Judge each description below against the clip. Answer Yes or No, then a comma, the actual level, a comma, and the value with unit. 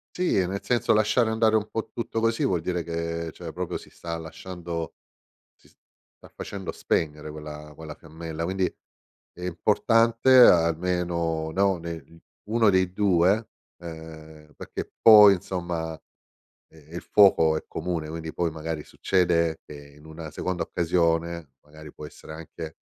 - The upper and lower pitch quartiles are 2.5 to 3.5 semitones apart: Yes, average, 2.9 semitones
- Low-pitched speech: Yes, very low, 85 Hz